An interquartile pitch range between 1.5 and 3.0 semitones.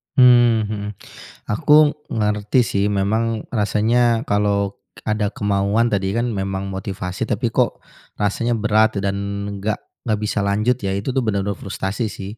Yes: narrow, 2.5 semitones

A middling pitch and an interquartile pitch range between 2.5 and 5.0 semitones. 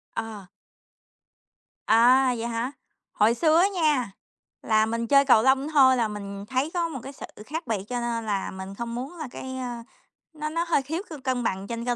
No: very high, 250 Hz; average, 3.9 semitones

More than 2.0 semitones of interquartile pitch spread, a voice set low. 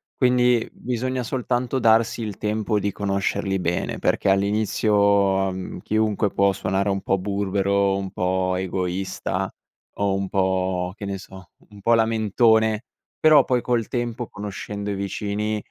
Yes: narrow, 2.4 semitones; low, 100 Hz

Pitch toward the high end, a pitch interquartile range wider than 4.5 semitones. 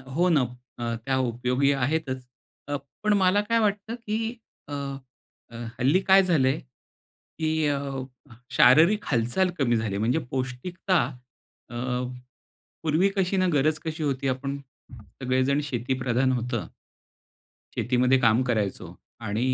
No: low, 135 Hz; wide, 5.4 semitones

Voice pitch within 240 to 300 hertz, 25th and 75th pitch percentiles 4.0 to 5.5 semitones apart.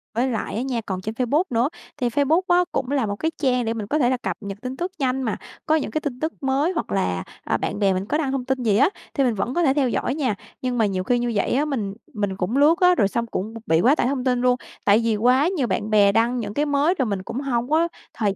Yes: very high, 250 Hz; average, 4.7 semitones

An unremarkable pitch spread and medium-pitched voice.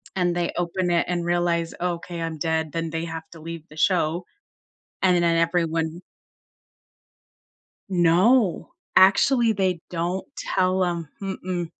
No: narrow, 1.7 semitones; medium, 175 Hz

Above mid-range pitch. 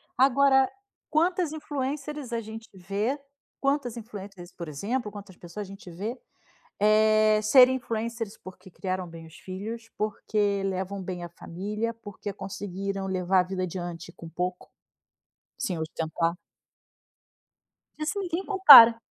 Yes: high, 210 Hz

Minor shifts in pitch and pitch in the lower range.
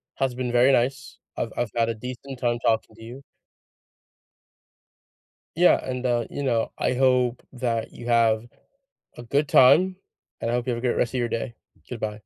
Yes: narrow, 1.8 semitones; low, 120 Hz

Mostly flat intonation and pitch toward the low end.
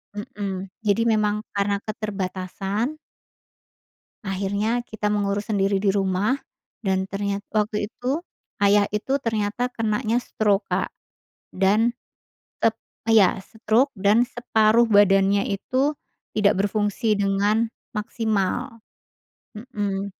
No: narrow, 2.2 semitones; high, 210 Hz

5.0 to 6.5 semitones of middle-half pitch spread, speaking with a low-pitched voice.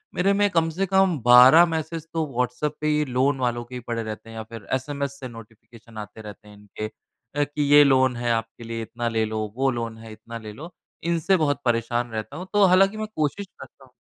Yes: wide, 5.4 semitones; low, 125 Hz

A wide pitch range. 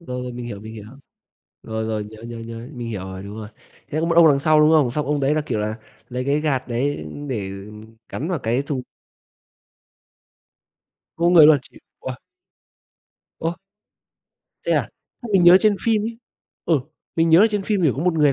Yes: wide, 6.1 semitones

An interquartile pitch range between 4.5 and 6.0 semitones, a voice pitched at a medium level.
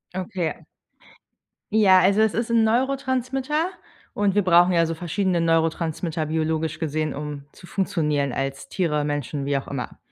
Yes: average, 5.0 semitones; medium, 170 Hz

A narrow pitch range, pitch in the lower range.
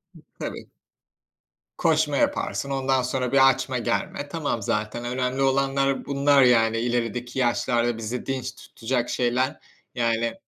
Yes: narrow, 2.2 semitones; low, 125 Hz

